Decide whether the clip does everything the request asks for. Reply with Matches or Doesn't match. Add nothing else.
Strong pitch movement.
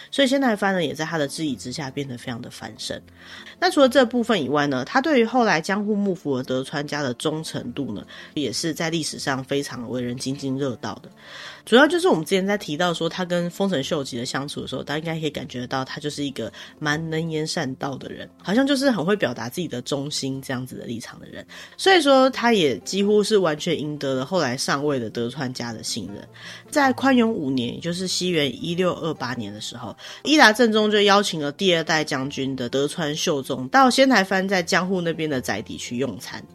Matches